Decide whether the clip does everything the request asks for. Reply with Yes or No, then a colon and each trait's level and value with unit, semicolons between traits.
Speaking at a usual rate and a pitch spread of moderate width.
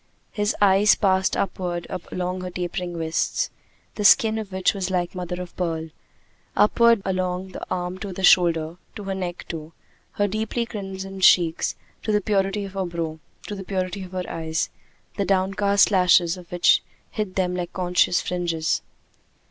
No: average, 165 wpm; narrow, 1.8 semitones